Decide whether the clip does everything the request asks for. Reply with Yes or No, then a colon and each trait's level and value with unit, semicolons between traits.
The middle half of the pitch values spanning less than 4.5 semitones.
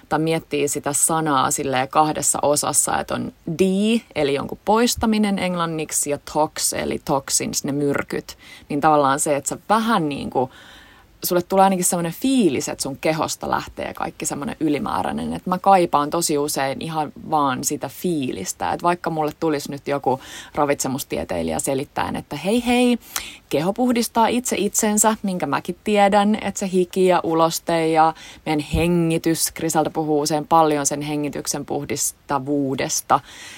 No: average, 4.8 semitones